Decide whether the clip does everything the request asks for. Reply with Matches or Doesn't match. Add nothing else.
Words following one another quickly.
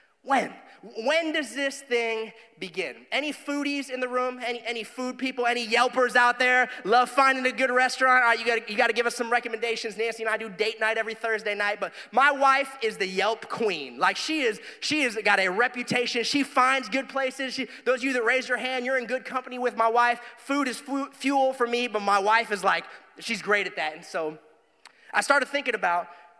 Matches